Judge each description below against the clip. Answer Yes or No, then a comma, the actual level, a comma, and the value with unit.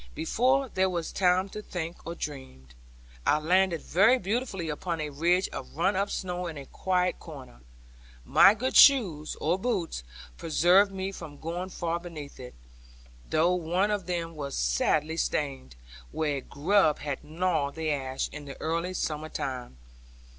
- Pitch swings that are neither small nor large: Yes, average, 3.9 semitones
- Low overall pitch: No, medium, 170 Hz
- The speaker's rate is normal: Yes, average, 160 wpm